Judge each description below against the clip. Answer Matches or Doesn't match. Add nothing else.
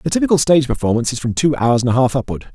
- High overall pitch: Doesn't match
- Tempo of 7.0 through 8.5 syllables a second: Matches